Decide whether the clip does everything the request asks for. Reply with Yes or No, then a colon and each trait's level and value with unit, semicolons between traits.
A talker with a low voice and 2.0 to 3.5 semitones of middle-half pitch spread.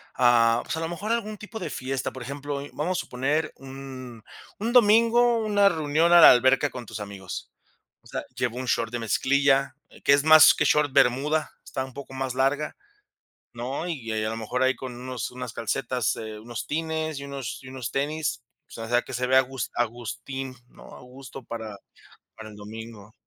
No: low, 130 Hz; average, 3.9 semitones